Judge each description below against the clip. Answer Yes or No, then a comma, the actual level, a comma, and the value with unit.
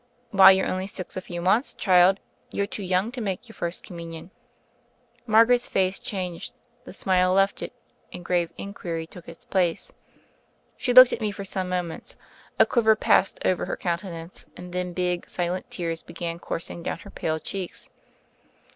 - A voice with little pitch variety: Yes, narrow, 2.3 semitones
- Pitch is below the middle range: No, medium, 185 Hz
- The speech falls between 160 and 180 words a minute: Yes, average, 175 wpm